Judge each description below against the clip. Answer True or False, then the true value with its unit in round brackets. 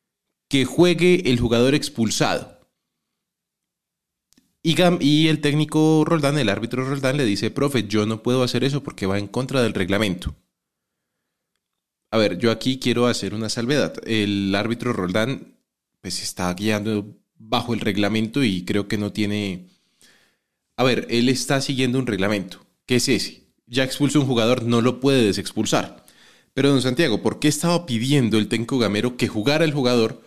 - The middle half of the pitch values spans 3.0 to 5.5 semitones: True (4.5 semitones)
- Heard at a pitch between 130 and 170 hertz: False (120 Hz)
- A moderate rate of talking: True (160 wpm)